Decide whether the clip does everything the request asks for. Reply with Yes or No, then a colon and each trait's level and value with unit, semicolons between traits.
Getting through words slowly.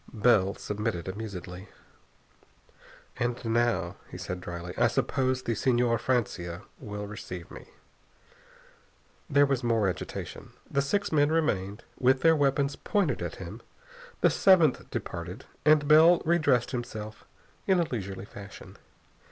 Yes: slow, 130 wpm